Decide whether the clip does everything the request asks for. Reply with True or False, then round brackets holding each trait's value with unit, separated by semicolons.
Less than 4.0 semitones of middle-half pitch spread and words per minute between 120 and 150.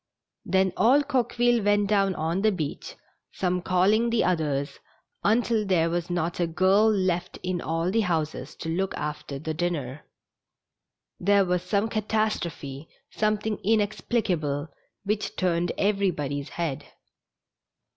False (4.4 semitones; 135 wpm)